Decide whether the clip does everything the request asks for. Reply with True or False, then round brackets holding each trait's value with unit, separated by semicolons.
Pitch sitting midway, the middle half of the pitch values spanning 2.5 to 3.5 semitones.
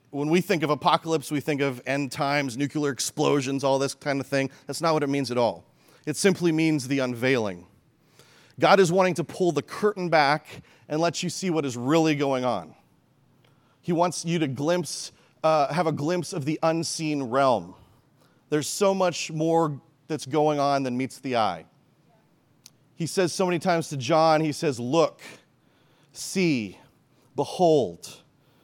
True (150 Hz; 3.2 semitones)